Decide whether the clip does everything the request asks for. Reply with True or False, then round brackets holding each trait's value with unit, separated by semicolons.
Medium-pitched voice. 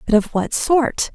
False (255 Hz)